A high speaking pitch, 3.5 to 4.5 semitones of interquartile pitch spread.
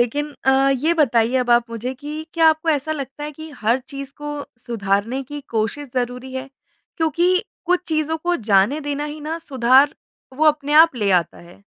Yes: very high, 280 Hz; average, 4.2 semitones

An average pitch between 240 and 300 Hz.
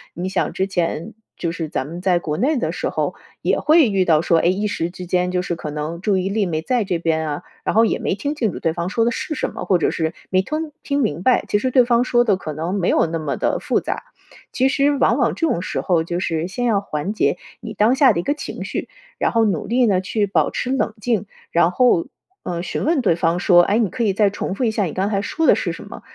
No: high, 195 Hz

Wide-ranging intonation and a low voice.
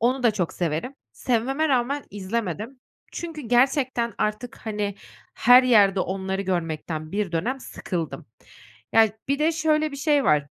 No: wide, 5.9 semitones; high, 230 Hz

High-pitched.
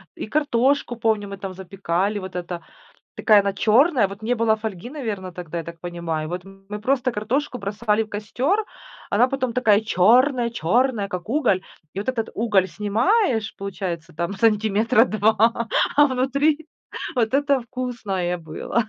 Yes: high, 215 Hz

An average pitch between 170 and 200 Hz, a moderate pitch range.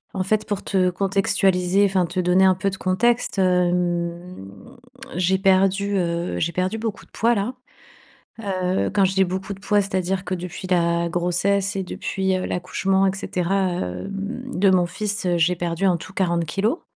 No: medium, 185 Hz; narrow, 1.8 semitones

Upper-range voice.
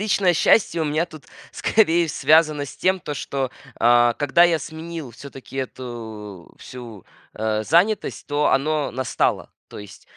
No: medium, 145 Hz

